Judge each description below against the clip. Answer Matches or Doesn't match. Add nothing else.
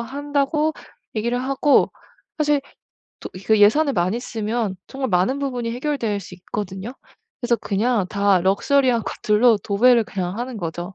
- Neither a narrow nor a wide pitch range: Matches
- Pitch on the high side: Matches